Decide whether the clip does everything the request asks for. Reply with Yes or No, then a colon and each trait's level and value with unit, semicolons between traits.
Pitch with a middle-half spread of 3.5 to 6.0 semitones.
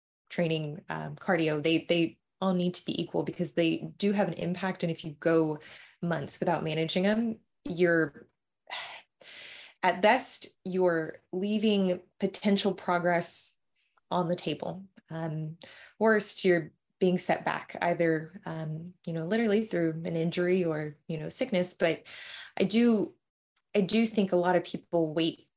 No: average, 3.1 semitones